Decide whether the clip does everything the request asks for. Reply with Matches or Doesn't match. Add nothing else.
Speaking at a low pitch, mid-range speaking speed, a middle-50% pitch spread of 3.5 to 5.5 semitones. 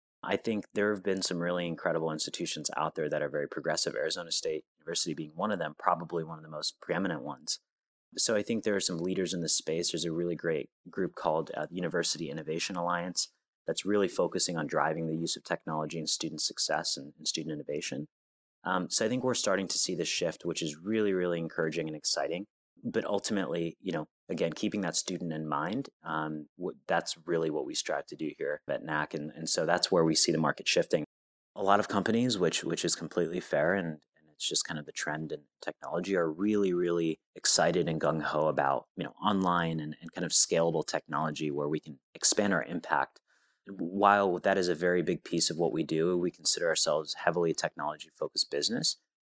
Doesn't match